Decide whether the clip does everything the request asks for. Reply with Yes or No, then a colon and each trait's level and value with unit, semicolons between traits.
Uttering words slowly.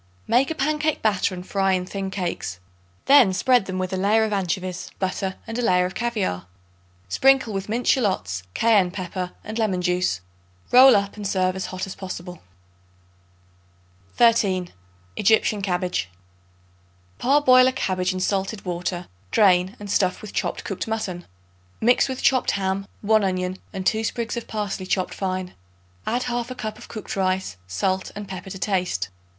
No: average, 160 wpm